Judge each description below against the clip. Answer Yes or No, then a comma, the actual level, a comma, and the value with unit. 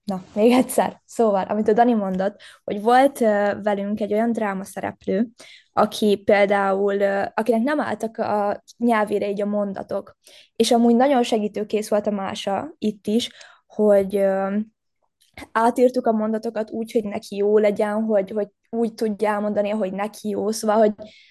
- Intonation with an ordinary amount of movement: No, narrow, 1.9 semitones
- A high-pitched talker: Yes, high, 215 Hz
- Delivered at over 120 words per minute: Yes, average, 150 wpm